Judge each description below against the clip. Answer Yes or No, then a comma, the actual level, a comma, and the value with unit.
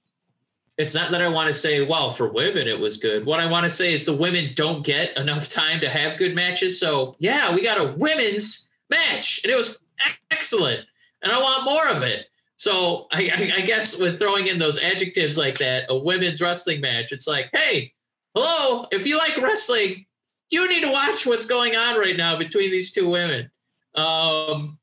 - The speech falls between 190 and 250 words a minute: Yes, average, 200 wpm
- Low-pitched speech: No, medium, 185 Hz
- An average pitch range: No, wide, 7.9 semitones